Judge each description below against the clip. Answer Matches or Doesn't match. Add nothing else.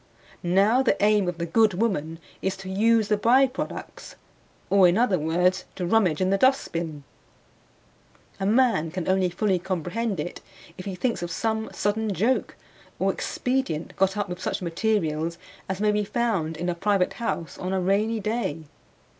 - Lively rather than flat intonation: Doesn't match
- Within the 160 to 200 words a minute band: Matches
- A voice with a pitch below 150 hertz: Doesn't match